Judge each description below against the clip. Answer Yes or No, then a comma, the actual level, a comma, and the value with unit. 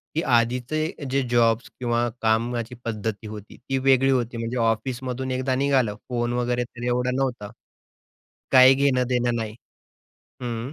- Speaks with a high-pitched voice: No, low, 125 Hz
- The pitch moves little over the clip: Yes, narrow, 2.0 semitones